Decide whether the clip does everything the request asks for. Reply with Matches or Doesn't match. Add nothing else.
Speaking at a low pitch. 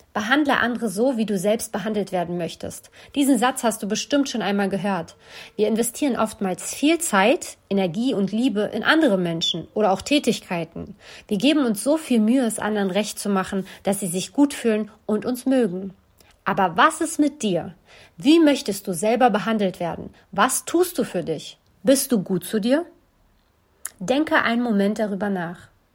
Doesn't match